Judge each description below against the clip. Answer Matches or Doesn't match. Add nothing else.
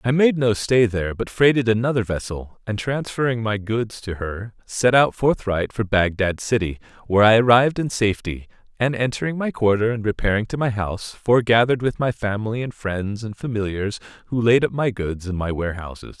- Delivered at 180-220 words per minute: Matches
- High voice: Doesn't match